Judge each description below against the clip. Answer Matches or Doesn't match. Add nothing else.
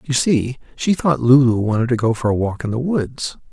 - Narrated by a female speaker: Doesn't match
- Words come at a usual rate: Doesn't match